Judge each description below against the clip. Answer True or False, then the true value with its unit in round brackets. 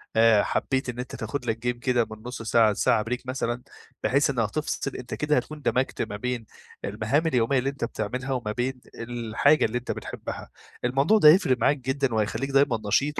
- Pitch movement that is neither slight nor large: True (3.1 semitones)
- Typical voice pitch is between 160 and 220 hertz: False (125 Hz)